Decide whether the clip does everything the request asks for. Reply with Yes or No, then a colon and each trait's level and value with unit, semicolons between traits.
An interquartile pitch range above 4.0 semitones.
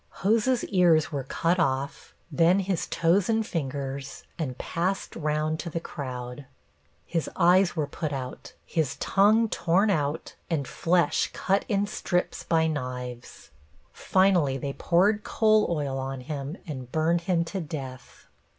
Yes: average, 5.1 semitones